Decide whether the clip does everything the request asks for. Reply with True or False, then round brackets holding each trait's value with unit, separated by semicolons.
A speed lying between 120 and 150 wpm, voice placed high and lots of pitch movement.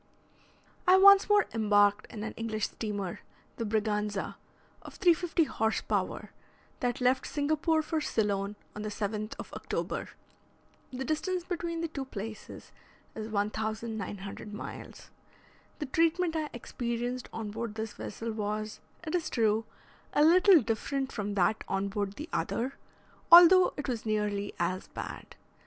True (140 wpm; 225 Hz; 6.8 semitones)